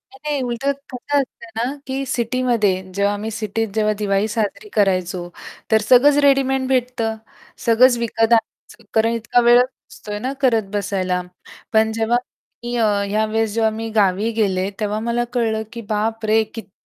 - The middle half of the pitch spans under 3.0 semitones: Yes, narrow, 2.6 semitones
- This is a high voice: Yes, high, 225 Hz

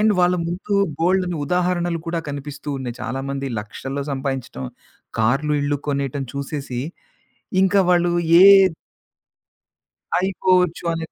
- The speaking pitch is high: No, medium, 150 Hz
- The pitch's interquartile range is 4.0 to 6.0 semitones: Yes, average, 4.6 semitones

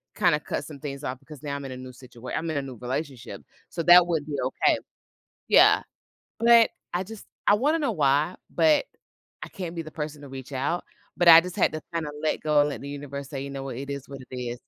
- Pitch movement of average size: Yes, average, 3.6 semitones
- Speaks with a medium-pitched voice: Yes, medium, 145 Hz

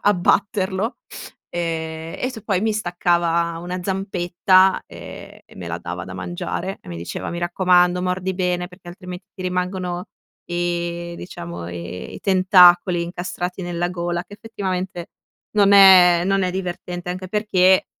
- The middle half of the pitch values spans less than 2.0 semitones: Yes, narrow, 1.5 semitones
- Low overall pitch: No, medium, 180 Hz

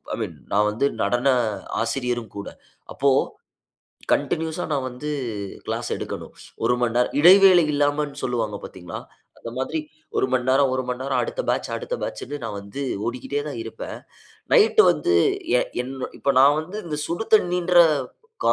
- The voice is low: Yes, low, 130 Hz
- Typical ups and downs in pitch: Yes, average, 3.9 semitones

